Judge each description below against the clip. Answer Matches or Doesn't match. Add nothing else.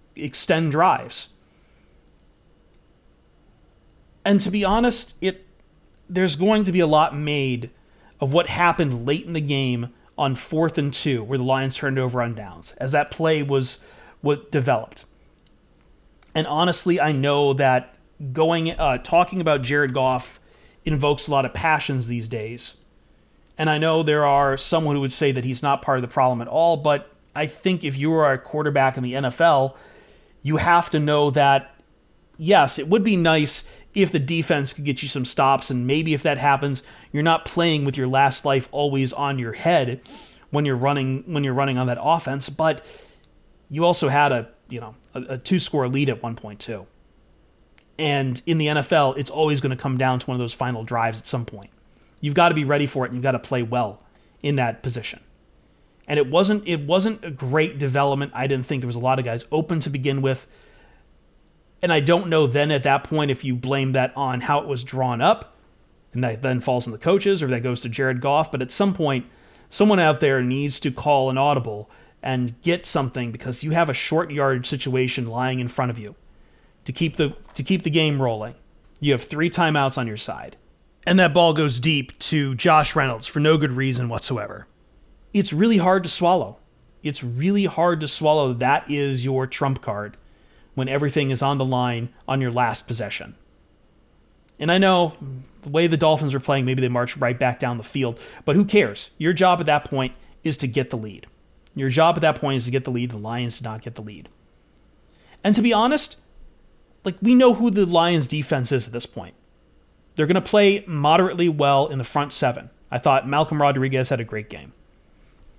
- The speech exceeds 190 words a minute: Matches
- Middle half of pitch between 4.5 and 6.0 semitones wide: Doesn't match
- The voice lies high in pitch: Doesn't match